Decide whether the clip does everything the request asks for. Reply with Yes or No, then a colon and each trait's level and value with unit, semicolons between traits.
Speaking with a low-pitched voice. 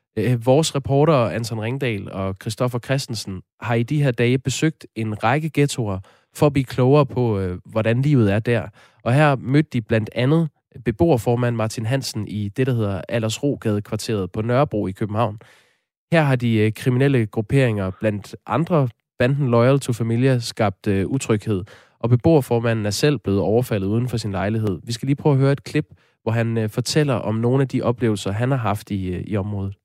Yes: low, 120 Hz